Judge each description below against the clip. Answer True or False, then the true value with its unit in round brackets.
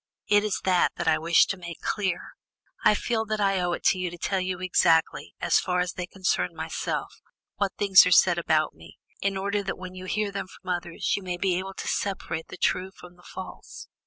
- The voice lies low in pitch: False (185 Hz)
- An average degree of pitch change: False (1.8 semitones)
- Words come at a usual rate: False (225 wpm)